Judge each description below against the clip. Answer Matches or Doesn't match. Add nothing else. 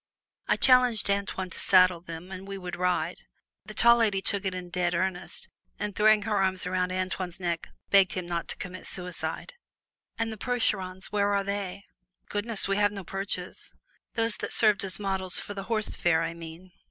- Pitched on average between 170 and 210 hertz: Matches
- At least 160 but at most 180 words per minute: Doesn't match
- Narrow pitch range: Matches